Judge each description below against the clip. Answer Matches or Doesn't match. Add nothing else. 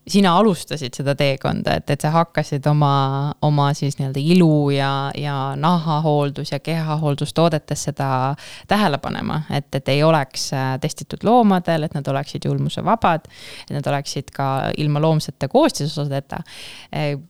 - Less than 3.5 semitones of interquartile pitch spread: Matches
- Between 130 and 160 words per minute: Matches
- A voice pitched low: Doesn't match